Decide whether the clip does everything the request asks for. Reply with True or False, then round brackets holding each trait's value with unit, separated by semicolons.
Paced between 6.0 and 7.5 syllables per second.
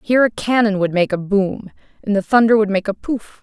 False (5.7 syllables/s)